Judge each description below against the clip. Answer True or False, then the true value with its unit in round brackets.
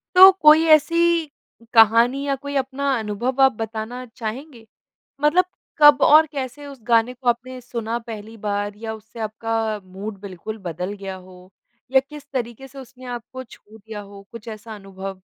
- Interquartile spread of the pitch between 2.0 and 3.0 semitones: False (4.1 semitones)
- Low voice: False (230 Hz)